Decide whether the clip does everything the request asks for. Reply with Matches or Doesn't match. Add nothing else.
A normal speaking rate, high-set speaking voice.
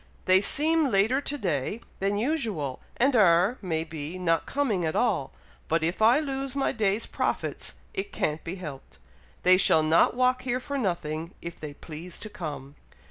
Matches